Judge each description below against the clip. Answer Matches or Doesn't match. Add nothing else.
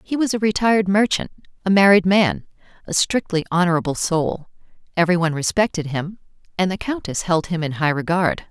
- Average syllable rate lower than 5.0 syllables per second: Doesn't match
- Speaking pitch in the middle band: Matches